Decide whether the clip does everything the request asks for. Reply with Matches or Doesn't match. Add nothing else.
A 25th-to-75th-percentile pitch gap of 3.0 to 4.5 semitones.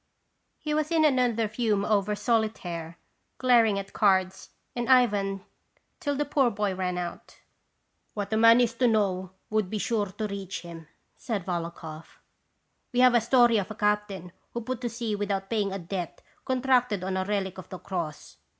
Matches